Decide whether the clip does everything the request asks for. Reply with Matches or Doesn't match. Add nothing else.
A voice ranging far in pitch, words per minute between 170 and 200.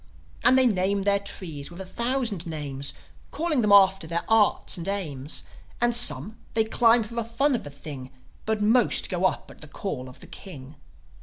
Matches